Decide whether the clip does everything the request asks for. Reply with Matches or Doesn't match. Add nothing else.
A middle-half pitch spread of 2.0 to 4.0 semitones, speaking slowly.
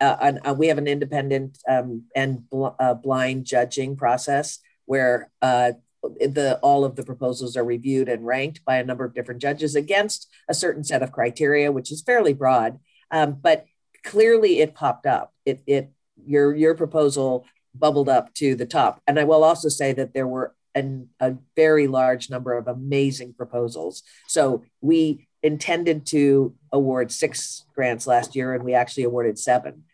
Doesn't match